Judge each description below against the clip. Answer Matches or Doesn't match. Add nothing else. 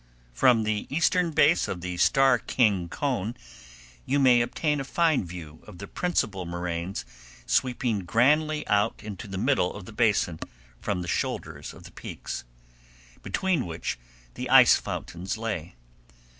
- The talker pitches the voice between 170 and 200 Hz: Doesn't match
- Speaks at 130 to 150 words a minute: Matches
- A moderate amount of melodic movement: Doesn't match